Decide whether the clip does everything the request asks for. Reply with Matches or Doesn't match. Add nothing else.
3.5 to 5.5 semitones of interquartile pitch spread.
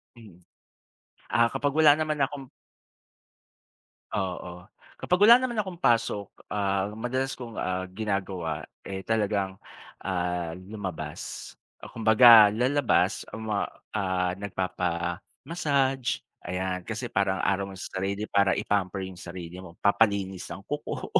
Matches